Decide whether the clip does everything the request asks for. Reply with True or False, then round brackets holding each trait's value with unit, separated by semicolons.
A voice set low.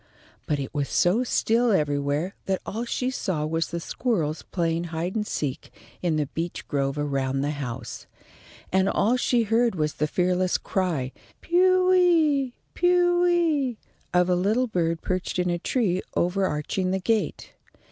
False (185 Hz)